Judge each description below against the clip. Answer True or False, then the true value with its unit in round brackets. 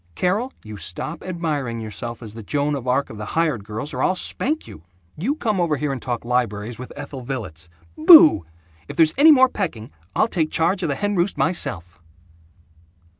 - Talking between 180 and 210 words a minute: True (190 wpm)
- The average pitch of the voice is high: False (145 Hz)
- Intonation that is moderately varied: False (8.1 semitones)